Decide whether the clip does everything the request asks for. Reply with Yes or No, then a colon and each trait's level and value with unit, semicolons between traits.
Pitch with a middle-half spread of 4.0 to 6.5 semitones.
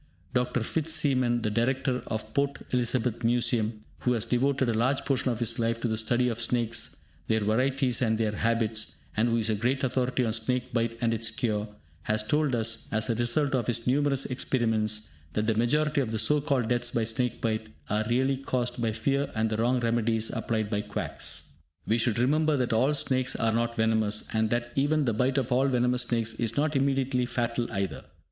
No: narrow, 2.5 semitones